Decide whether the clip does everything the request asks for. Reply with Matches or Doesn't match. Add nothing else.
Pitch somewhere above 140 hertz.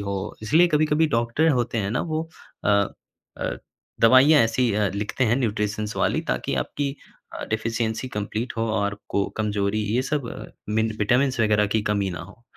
Doesn't match